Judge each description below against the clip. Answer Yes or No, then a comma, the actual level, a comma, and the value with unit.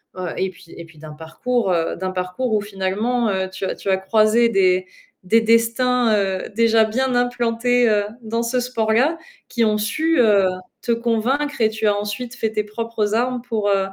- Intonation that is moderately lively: Yes, average, 3.6 semitones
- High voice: Yes, high, 220 Hz